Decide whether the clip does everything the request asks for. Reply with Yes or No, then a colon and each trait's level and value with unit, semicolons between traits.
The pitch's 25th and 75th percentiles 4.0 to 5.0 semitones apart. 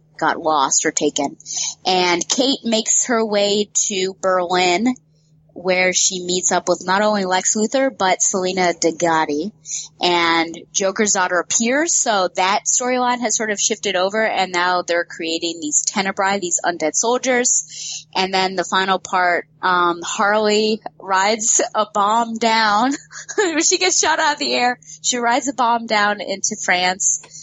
Yes: average, 4.5 semitones